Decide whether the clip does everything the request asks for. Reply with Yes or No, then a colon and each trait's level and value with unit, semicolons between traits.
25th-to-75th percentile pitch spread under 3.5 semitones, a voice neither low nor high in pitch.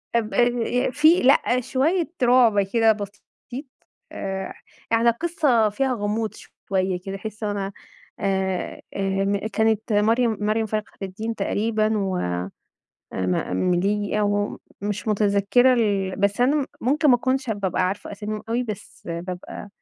No: average, 3.1 semitones; high, 210 Hz